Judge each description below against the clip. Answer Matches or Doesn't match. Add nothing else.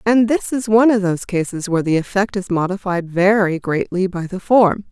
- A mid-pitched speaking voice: Doesn't match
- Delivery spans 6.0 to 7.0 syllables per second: Doesn't match